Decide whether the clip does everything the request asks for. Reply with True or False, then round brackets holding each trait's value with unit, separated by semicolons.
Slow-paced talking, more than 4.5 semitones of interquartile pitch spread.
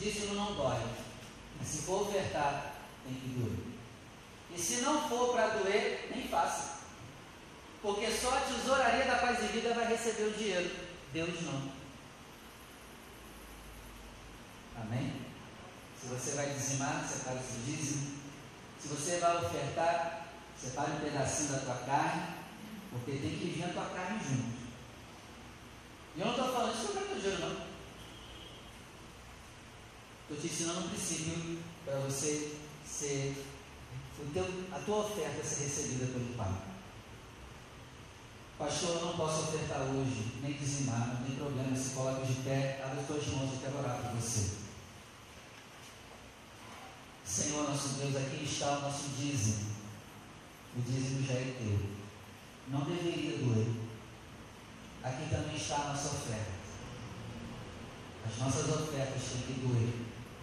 False (140 wpm; 5.1 semitones)